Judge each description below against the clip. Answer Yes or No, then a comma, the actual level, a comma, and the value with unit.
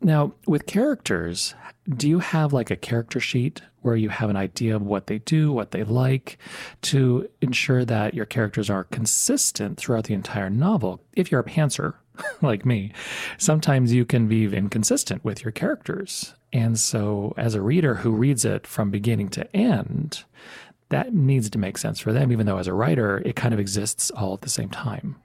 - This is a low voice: Yes, low, 120 Hz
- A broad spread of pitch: Yes, wide, 5.8 semitones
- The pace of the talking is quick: No, average, 190 wpm